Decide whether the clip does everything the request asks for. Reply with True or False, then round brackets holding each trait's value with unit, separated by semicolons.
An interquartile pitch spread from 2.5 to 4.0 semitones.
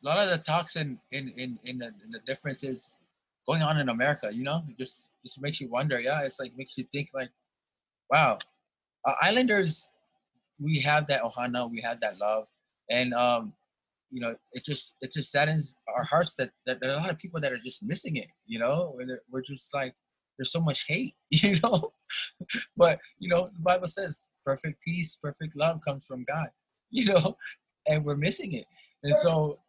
False (4.7 semitones)